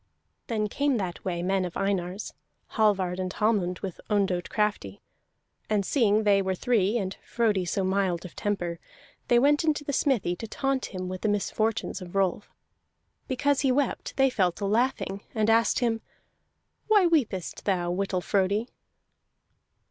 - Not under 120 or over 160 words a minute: Yes, average, 155 wpm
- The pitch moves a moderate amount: Yes, average, 3.9 semitones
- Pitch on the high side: Yes, high, 205 Hz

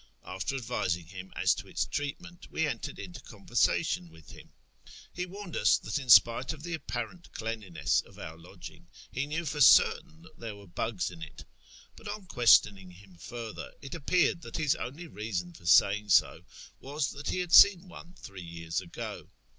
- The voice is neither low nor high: No, low, 120 Hz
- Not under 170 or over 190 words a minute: Yes, average, 180 wpm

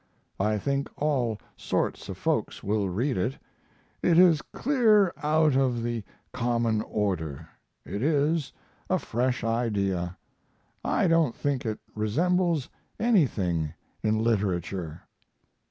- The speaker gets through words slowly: Yes, slow, 115 wpm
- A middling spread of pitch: No, wide, 6.6 semitones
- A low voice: Yes, low, 120 Hz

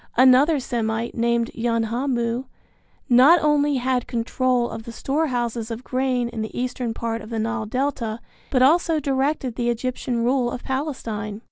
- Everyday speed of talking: Yes, average, 150 wpm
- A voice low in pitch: No, high, 245 Hz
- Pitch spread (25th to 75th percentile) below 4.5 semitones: Yes, narrow, 2.4 semitones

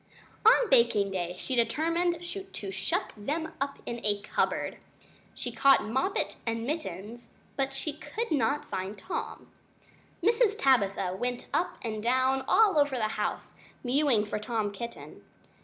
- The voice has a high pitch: Yes, very high, 250 Hz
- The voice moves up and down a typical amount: No, wide, 6.3 semitones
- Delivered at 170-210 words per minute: No, average, 140 wpm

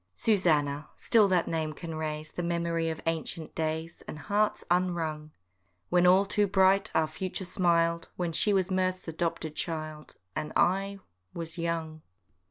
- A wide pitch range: No, average, 2.8 semitones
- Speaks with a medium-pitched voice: Yes, medium, 170 Hz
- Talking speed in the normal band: Yes, average, 155 wpm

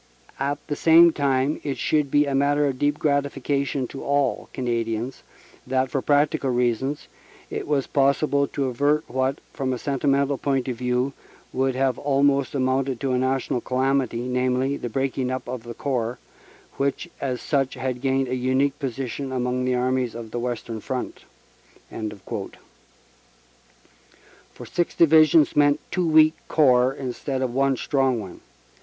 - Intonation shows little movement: Yes, narrow, 2.1 semitones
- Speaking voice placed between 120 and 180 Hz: Yes, low, 135 Hz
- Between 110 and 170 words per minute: Yes, average, 150 wpm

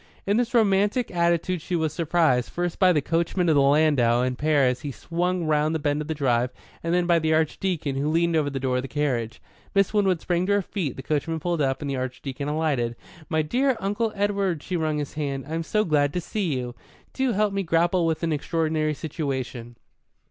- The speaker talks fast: Yes, fast, 220 wpm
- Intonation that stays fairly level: No, average, 4.0 semitones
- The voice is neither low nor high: Yes, medium, 160 Hz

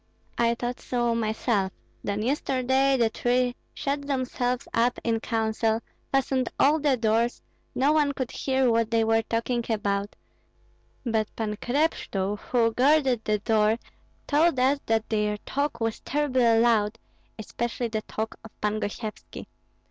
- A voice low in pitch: No, high, 235 Hz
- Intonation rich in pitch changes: No, average, 2.9 semitones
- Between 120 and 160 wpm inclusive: Yes, average, 140 wpm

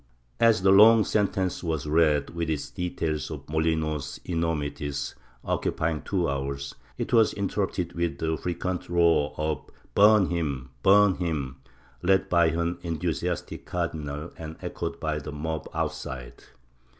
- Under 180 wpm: Yes, slow, 135 wpm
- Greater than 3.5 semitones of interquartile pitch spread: No, average, 3.0 semitones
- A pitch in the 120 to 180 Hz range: No, very low, 80 Hz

